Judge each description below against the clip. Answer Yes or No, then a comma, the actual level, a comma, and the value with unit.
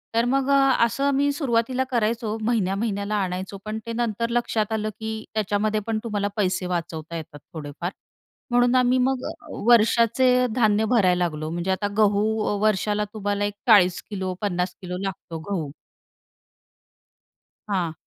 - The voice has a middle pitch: No, high, 210 Hz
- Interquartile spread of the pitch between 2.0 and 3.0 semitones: No, average, 3.9 semitones